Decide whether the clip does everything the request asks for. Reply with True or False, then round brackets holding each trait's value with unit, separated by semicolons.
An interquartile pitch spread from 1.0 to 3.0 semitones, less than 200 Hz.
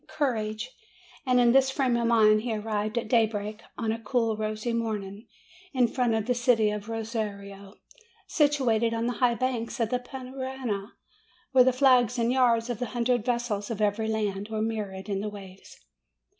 False (2.6 semitones; 225 Hz)